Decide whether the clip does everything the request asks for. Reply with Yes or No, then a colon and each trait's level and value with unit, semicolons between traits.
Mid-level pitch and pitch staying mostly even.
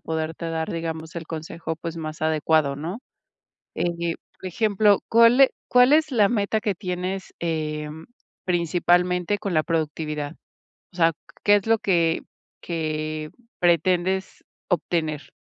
No: medium, 170 Hz; average, 3.2 semitones